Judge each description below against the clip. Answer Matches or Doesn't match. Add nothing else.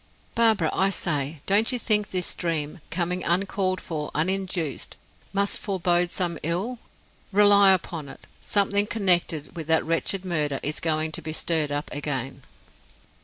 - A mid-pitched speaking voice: Matches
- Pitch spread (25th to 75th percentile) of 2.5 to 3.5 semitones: Doesn't match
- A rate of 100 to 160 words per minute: Matches